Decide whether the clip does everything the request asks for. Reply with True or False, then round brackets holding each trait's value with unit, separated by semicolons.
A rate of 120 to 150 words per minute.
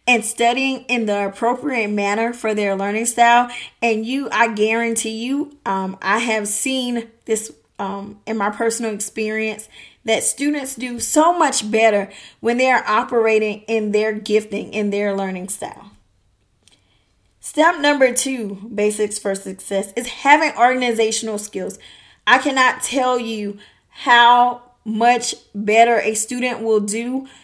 True (140 wpm)